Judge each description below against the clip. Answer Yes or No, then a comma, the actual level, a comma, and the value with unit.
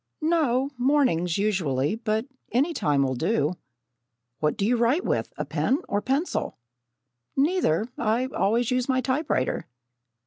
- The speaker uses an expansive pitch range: Yes, wide, 6.9 semitones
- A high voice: Yes, high, 235 Hz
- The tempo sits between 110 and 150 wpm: Yes, average, 140 wpm